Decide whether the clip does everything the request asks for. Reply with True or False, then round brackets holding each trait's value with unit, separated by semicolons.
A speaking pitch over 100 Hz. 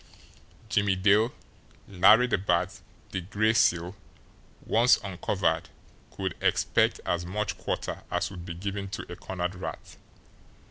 False (95 Hz)